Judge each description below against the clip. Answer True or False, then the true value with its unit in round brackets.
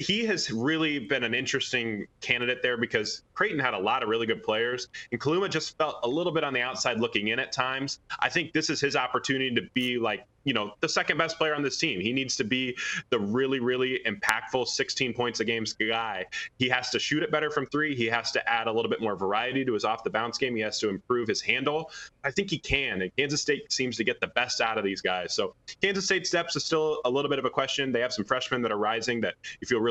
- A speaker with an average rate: False (260 wpm)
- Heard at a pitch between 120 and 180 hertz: True (135 Hz)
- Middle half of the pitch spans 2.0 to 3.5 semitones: False (4.1 semitones)